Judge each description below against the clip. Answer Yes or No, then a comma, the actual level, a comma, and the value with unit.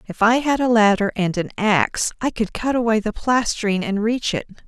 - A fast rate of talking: Yes, fast, 220 wpm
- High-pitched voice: Yes, high, 220 Hz